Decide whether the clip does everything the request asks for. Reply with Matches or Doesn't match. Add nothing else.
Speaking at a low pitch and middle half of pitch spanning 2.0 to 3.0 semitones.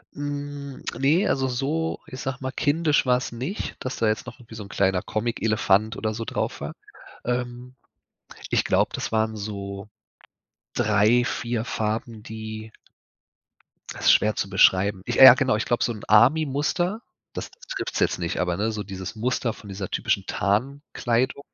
Doesn't match